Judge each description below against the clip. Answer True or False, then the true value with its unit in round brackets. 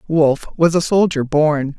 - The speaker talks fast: False (170 wpm)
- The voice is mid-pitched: True (155 Hz)